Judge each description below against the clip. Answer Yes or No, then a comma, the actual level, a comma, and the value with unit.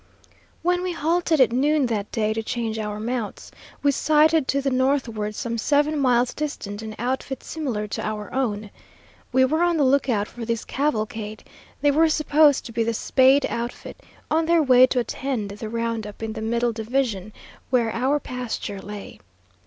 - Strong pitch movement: No, average, 4.5 semitones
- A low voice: No, high, 245 Hz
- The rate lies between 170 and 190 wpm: Yes, average, 175 wpm